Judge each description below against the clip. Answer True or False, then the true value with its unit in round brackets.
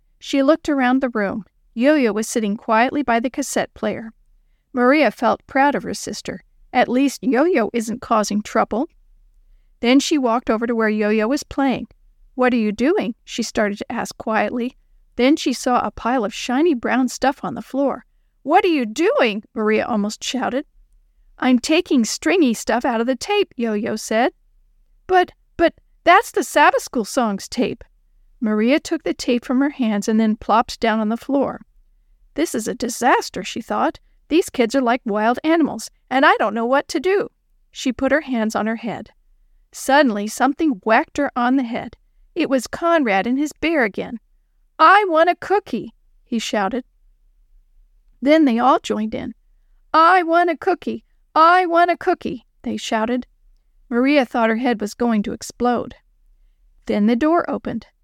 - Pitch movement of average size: True (4.8 semitones)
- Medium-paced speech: True (175 wpm)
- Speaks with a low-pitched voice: False (255 Hz)